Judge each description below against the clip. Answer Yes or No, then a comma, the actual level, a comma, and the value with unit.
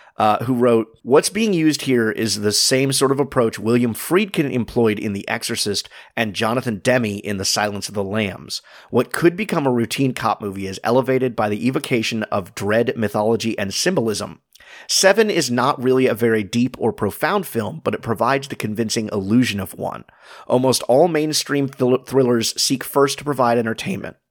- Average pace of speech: Yes, average, 180 wpm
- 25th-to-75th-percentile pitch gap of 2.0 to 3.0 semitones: No, average, 3.8 semitones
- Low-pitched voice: Yes, low, 120 Hz